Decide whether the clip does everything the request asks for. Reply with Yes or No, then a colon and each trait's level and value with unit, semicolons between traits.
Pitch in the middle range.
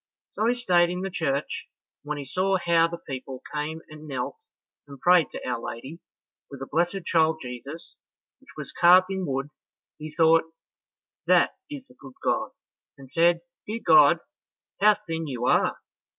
Yes: medium, 160 Hz